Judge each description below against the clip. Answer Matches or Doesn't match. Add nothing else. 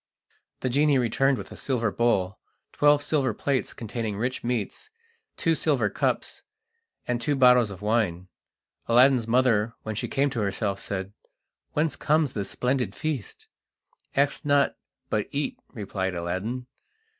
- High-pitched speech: Doesn't match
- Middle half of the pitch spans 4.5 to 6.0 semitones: Matches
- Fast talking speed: Doesn't match